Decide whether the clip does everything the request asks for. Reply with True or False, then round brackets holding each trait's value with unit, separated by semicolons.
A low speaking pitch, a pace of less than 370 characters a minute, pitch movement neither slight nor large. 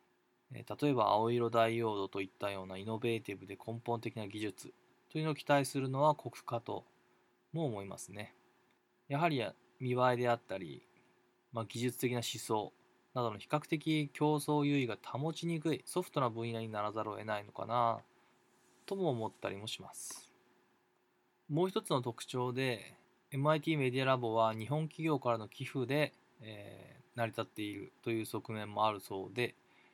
True (120 Hz; 320 characters per minute; 4.6 semitones)